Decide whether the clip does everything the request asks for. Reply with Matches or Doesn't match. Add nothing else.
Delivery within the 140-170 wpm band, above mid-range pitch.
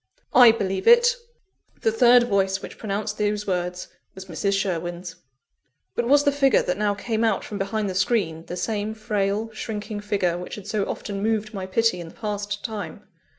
Doesn't match